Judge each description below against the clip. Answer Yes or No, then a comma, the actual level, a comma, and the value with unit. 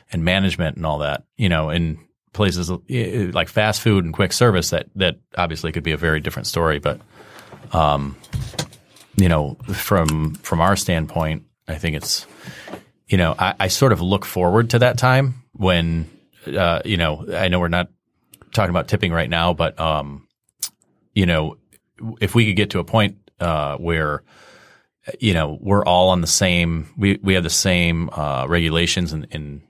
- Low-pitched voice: Yes, very low, 85 Hz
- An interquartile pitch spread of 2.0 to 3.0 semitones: No, average, 3.8 semitones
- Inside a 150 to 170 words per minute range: No, average, 180 wpm